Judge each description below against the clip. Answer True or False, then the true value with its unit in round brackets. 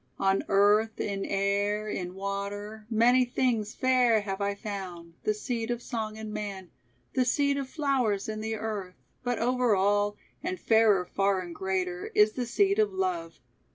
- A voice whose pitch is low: False (210 Hz)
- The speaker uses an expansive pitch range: False (2.6 semitones)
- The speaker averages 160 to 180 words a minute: True (165 wpm)